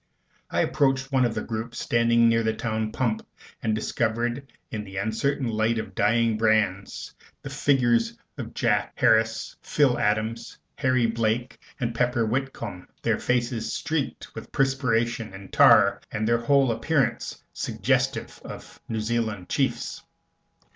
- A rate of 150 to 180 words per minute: No, average, 140 wpm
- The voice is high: No, low, 115 Hz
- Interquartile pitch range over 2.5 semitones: No, narrow, 2.0 semitones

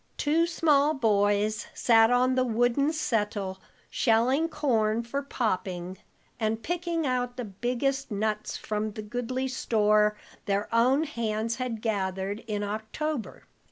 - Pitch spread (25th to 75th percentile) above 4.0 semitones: No, average, 3.7 semitones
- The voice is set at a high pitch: Yes, high, 230 Hz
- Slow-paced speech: Yes, slow, 125 wpm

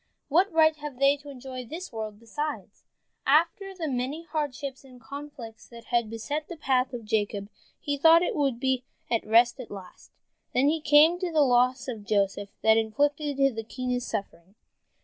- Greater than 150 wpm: Yes, average, 170 wpm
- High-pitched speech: Yes, very high, 260 Hz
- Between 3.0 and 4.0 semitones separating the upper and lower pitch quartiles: No, average, 4.5 semitones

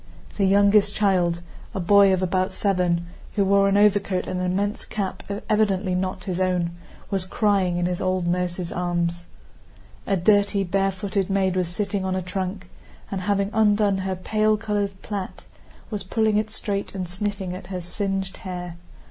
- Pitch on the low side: No, high, 190 Hz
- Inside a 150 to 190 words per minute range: Yes, average, 165 wpm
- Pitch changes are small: Yes, narrow, 1.9 semitones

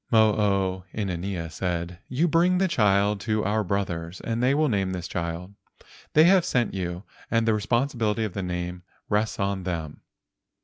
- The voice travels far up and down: No, average, 4.1 semitones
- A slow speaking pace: No, average, 175 wpm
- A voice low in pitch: Yes, low, 100 Hz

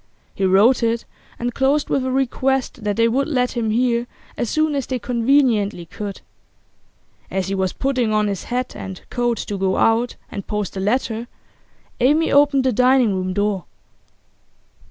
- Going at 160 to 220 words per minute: Yes, average, 170 wpm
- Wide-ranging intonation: No, average, 4.2 semitones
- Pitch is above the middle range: Yes, high, 235 Hz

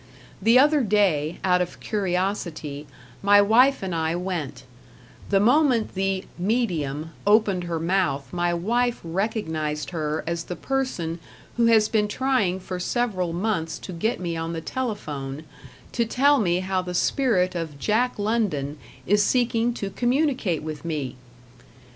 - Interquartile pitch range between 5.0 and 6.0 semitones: Yes, wide, 5.5 semitones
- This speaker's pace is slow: No, average, 145 wpm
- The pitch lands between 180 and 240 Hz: Yes, medium, 185 Hz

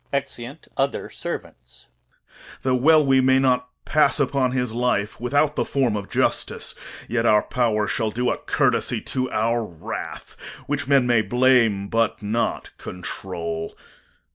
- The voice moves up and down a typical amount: Yes, average, 3.7 semitones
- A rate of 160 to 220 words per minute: No, average, 140 wpm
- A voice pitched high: No, low, 125 Hz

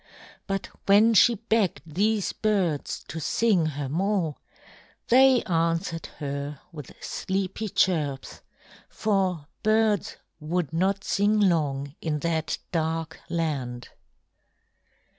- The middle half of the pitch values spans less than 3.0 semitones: No, average, 4.8 semitones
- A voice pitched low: No, medium, 170 Hz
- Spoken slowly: Yes, slow, 105 wpm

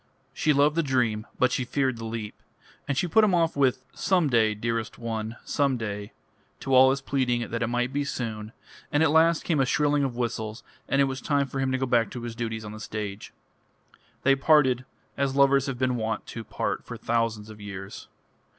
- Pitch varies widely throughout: No, average, 3.7 semitones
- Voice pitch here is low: Yes, low, 125 Hz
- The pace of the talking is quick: Yes, fast, 215 wpm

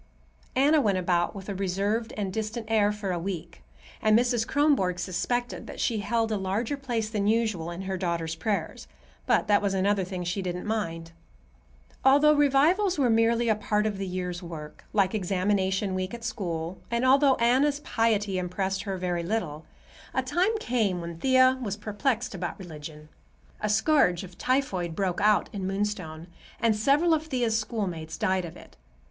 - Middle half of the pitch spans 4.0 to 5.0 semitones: Yes, average, 4.5 semitones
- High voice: Yes, high, 205 Hz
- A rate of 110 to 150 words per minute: No, average, 175 wpm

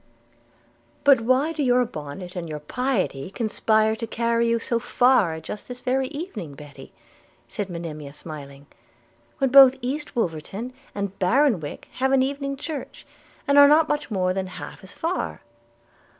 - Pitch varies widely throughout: Yes, wide, 7.0 semitones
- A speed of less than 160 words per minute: Yes, average, 150 wpm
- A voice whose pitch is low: No, high, 230 Hz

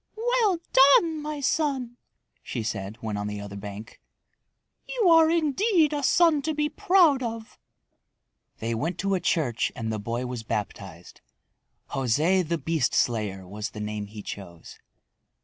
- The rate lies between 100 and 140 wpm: No, average, 150 wpm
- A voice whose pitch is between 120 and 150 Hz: No, medium, 160 Hz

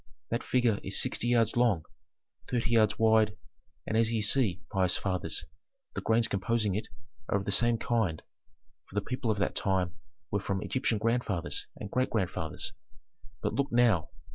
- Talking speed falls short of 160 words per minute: No, average, 165 wpm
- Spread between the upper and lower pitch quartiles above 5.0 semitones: No, average, 3.2 semitones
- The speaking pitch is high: No, low, 110 Hz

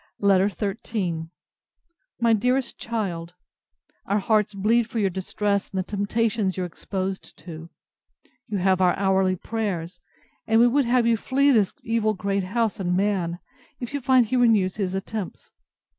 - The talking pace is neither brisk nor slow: Yes, average, 160 wpm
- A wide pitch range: No, average, 3.4 semitones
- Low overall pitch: No, high, 200 Hz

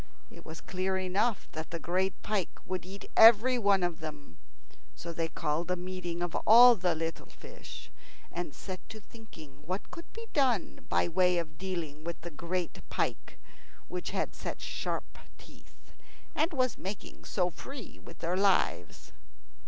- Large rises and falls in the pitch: No, average, 3.5 semitones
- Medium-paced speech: Yes, average, 160 wpm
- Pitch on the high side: No, medium, 180 Hz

